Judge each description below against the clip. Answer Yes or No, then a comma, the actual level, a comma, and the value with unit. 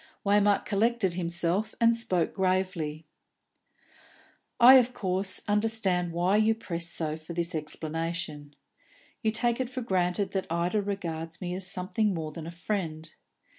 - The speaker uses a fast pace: No, average, 140 wpm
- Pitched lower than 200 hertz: Yes, medium, 185 Hz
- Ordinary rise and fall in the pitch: Yes, average, 3.8 semitones